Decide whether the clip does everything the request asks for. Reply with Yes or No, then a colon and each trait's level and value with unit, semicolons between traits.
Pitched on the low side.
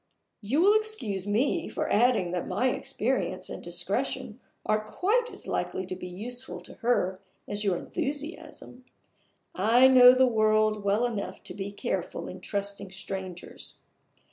No: high, 215 Hz